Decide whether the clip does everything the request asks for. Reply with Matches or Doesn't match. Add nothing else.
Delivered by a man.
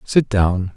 Matches